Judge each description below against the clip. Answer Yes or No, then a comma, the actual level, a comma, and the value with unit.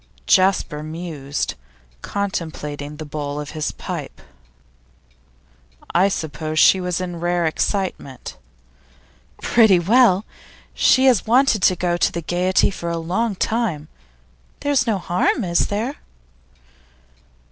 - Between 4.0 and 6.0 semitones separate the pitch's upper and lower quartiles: Yes, average, 4.4 semitones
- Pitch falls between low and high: Yes, medium, 175 Hz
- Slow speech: Yes, slow, 115 wpm